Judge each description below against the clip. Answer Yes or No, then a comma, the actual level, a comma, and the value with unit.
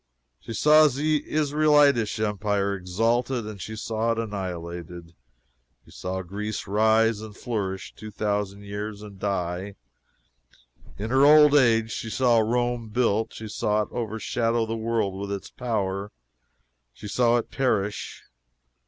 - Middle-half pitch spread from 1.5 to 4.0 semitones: Yes, average, 2.9 semitones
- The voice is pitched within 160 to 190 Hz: No, low, 110 Hz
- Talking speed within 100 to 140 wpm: Yes, slow, 135 wpm